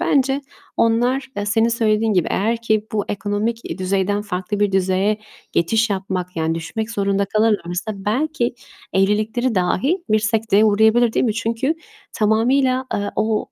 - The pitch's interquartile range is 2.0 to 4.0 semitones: Yes, narrow, 2.6 semitones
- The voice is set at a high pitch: Yes, high, 215 Hz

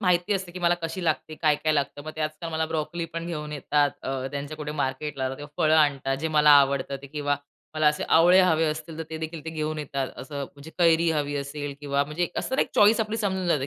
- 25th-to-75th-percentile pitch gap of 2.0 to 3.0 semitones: Yes, narrow, 2.5 semitones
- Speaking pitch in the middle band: Yes, medium, 155 Hz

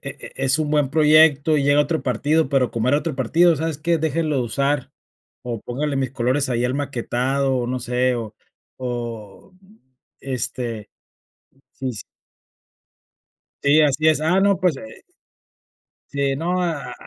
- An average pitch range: Yes, average, 3.6 semitones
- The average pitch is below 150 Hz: Yes, medium, 140 Hz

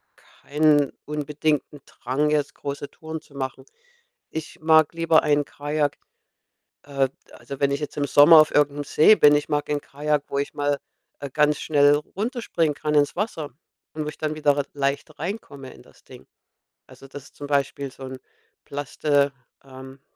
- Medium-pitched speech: Yes, medium, 145 Hz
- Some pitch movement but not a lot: No, narrow, 1.5 semitones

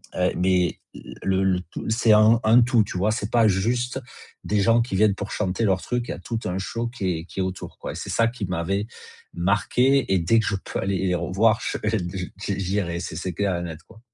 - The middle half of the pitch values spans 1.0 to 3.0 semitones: No, average, 3.7 semitones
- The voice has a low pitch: Yes, low, 100 Hz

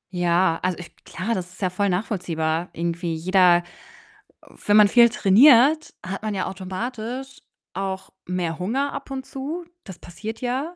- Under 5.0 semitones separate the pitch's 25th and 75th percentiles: No, wide, 5.4 semitones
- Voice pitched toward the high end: Yes, high, 195 Hz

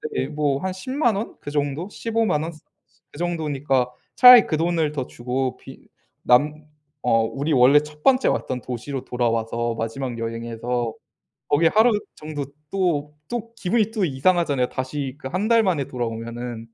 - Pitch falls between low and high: Yes, medium, 145 Hz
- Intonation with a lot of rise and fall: Yes, wide, 6.2 semitones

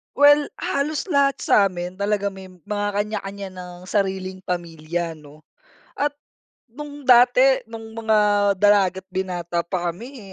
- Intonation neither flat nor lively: Yes, average, 4.9 semitones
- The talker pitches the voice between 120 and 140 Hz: No, high, 200 Hz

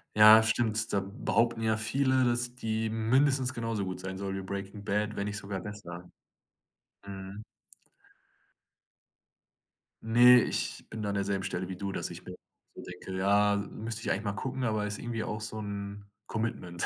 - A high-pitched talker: No, low, 105 Hz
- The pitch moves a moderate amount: No, narrow, 2.3 semitones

